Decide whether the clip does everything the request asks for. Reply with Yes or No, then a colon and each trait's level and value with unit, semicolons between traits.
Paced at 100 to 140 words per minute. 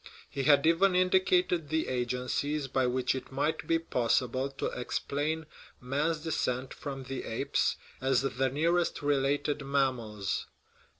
Yes: slow, 135 wpm